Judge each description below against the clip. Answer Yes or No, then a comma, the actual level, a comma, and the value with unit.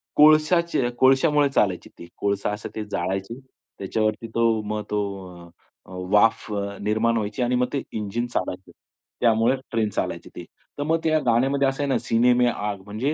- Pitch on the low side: Yes, low, 115 Hz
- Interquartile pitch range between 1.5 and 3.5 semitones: No, average, 4.3 semitones